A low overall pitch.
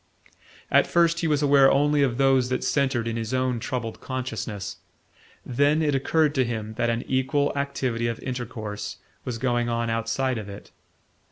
Yes: low, 130 Hz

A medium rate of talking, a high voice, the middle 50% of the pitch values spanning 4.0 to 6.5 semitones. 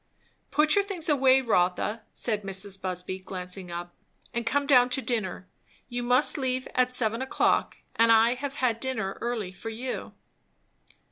Yes: average, 155 wpm; high, 235 Hz; average, 5.2 semitones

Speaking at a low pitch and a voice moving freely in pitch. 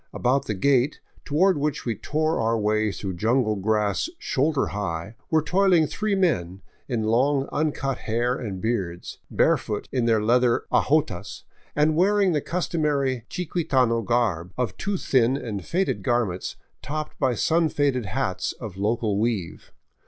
Yes: low, 125 Hz; wide, 6.0 semitones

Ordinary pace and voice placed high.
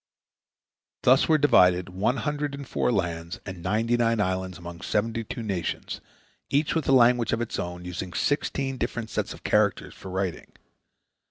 No: average, 170 wpm; low, 110 Hz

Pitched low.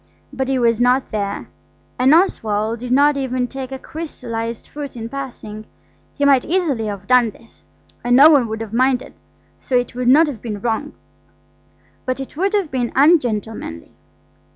No: very high, 250 Hz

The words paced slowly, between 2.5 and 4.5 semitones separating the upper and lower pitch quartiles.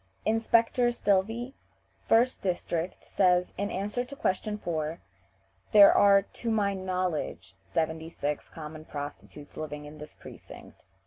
No: slow, 125 wpm; wide, 5.4 semitones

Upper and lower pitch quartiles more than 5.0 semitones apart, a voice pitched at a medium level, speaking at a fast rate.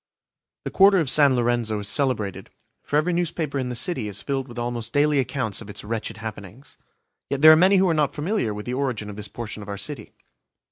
No: wide, 5.5 semitones; low, 125 Hz; fast, 225 wpm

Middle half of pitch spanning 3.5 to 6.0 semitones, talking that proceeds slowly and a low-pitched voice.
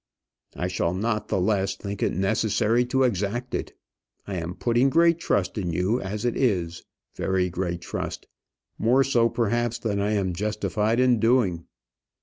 No: average, 4.1 semitones; average, 160 wpm; low, 105 Hz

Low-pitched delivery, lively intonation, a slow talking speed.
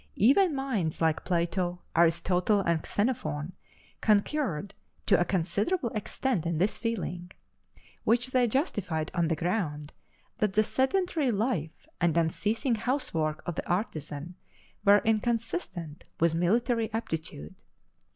No: high, 195 Hz; wide, 5.8 semitones; slow, 120 wpm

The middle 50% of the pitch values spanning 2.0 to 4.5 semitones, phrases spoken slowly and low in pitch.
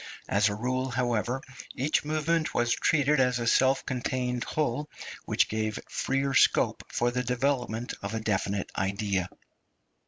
No: average, 3.5 semitones; average, 145 wpm; low, 125 Hz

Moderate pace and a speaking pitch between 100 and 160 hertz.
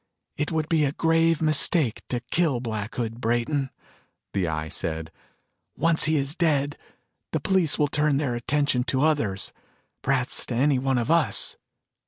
Yes: average, 160 wpm; medium, 140 Hz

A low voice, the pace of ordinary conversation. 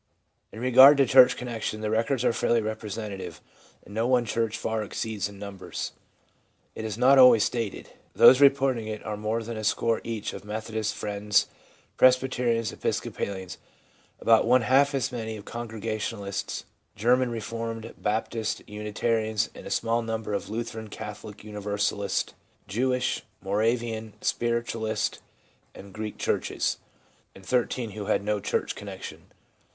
Yes: low, 110 Hz; average, 145 wpm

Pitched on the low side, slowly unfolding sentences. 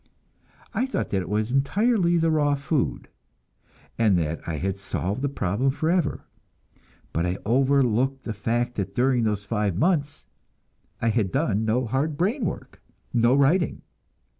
No: low, 125 Hz; average, 150 wpm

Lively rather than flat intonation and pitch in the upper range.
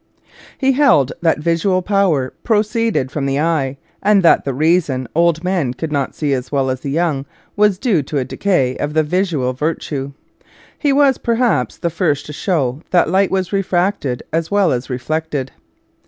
No: wide, 5.9 semitones; medium, 160 Hz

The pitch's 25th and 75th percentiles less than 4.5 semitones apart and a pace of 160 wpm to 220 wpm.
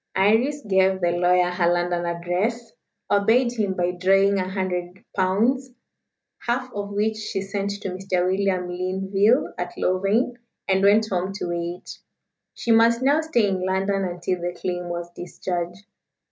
No: average, 3.0 semitones; average, 150 wpm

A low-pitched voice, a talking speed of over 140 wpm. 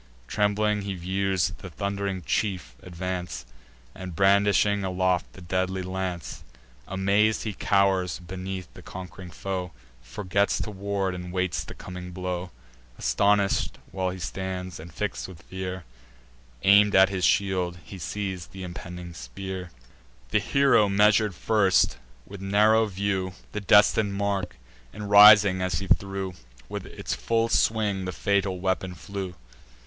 No: very low, 95 Hz; slow, 135 wpm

